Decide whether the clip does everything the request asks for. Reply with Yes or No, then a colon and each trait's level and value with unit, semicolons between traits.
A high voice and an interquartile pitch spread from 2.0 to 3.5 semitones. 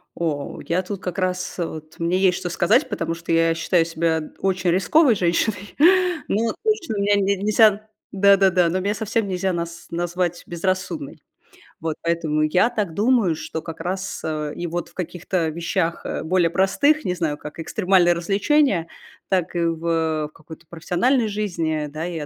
No: medium, 175 Hz; average, 2.9 semitones